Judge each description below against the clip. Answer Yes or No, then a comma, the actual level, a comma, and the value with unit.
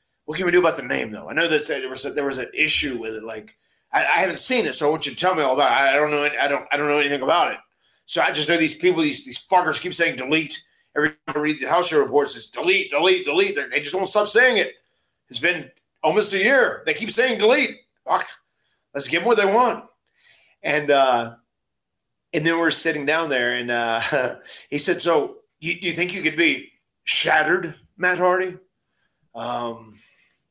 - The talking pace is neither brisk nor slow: No, fast, 230 wpm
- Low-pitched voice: No, medium, 165 Hz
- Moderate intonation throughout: No, wide, 6.8 semitones